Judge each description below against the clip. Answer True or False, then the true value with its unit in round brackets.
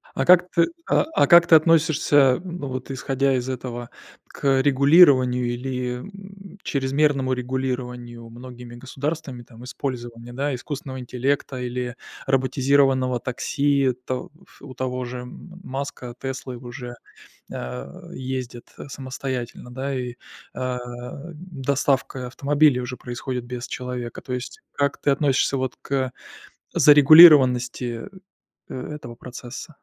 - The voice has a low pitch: True (130 Hz)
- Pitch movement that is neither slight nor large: False (2.2 semitones)